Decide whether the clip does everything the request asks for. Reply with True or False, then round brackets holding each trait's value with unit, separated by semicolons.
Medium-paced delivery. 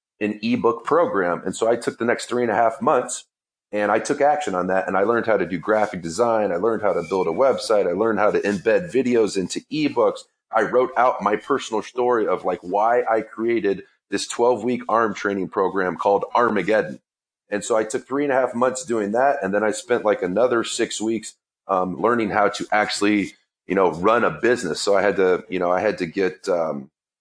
False (225 wpm)